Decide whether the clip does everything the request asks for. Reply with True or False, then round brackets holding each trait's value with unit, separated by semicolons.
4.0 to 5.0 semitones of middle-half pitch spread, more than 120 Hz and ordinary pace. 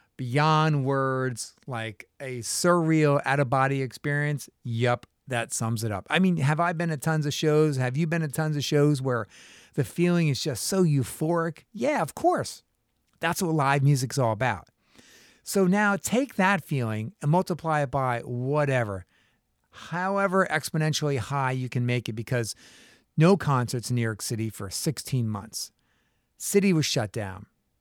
True (4.7 semitones; 140 Hz; 160 wpm)